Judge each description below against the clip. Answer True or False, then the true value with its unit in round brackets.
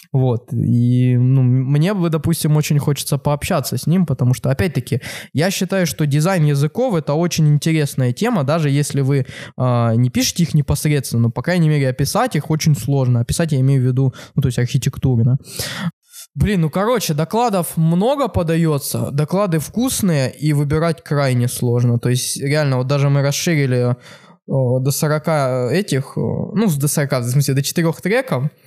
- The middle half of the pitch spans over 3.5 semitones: True (4.0 semitones)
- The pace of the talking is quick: True (165 wpm)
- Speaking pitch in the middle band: True (145 Hz)